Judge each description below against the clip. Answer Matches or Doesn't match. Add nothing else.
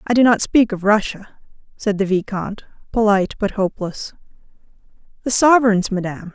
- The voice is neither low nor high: Doesn't match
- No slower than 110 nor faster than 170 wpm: Matches